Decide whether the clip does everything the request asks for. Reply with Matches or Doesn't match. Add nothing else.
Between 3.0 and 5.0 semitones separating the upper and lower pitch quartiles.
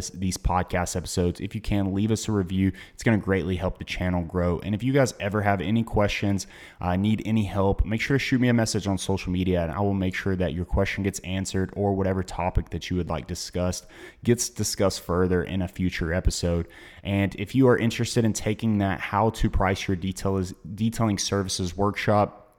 Doesn't match